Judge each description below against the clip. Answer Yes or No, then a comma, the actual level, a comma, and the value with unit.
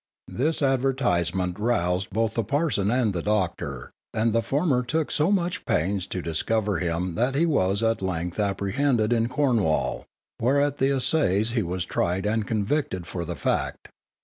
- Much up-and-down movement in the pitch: Yes, wide, 6.3 semitones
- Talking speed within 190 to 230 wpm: No, average, 165 wpm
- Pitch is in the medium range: No, low, 110 Hz